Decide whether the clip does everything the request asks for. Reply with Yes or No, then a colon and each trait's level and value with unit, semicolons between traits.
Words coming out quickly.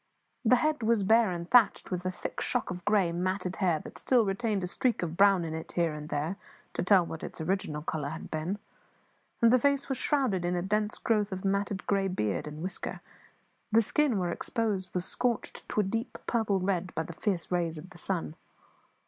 Yes: fast, 210 wpm